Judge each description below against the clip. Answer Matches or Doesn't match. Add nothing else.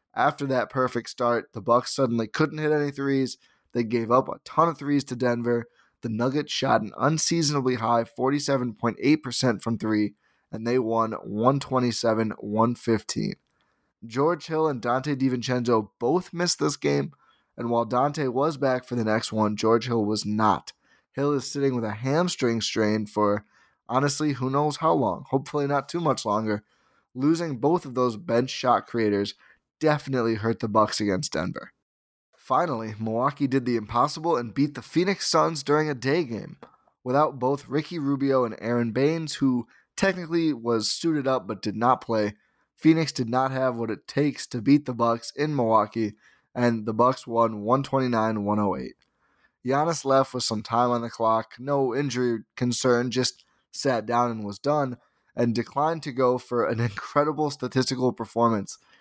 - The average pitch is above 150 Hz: Doesn't match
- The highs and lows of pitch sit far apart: Doesn't match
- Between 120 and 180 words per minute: Matches